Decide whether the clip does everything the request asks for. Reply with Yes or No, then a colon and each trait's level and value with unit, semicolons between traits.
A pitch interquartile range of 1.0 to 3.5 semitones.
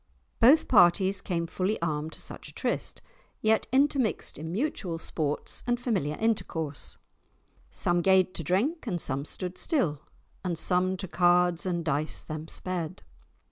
No: average, 4.6 semitones